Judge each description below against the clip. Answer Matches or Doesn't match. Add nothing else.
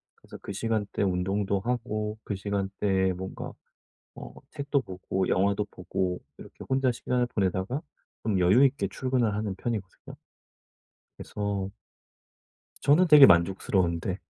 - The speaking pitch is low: Matches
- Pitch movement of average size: Matches